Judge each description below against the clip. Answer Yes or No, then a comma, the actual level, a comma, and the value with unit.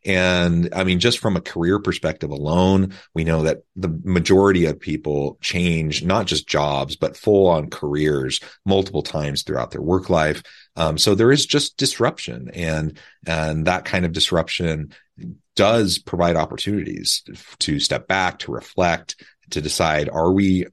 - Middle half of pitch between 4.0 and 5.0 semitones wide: No, average, 3.4 semitones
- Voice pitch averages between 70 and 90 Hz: Yes, very low, 85 Hz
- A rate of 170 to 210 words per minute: No, average, 155 wpm